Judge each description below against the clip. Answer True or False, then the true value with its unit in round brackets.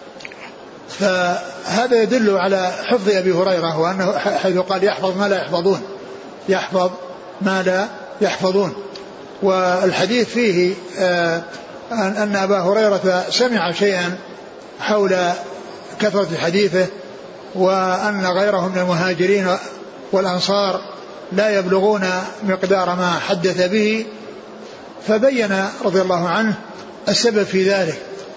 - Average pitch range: False (1.7 semitones)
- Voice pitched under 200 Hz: True (190 Hz)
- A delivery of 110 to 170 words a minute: False (95 wpm)